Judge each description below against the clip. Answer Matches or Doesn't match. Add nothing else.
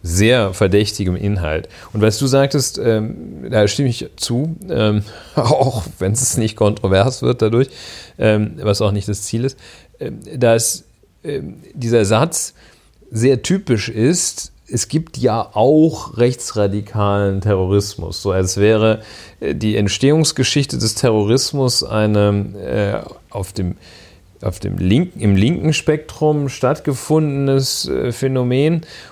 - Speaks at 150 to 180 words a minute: Doesn't match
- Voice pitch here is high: Doesn't match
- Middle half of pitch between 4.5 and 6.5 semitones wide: Matches